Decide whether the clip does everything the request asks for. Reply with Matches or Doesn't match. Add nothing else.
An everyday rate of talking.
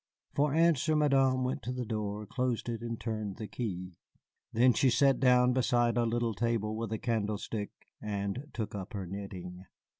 Matches